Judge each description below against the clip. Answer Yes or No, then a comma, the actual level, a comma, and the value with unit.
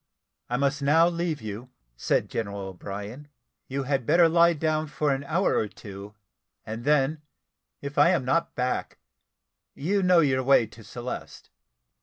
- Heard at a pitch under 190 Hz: Yes, medium, 140 Hz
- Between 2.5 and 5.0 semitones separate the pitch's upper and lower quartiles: No, wide, 5.5 semitones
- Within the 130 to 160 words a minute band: Yes, average, 155 wpm